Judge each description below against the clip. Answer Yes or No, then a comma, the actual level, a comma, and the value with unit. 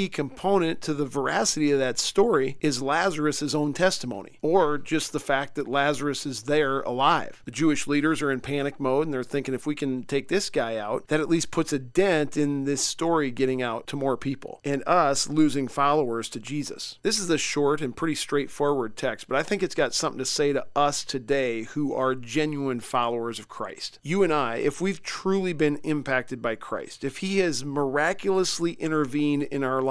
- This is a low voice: No, medium, 145 Hz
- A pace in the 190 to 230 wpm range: Yes, average, 200 wpm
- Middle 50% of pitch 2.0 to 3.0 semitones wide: Yes, narrow, 2.4 semitones